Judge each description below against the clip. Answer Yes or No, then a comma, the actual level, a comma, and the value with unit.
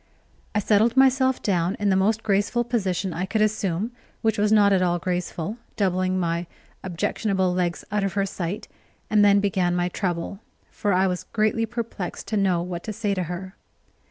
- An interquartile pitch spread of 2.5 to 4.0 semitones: Yes, average, 2.9 semitones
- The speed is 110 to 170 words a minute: No, average, 185 wpm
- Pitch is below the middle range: No, high, 195 Hz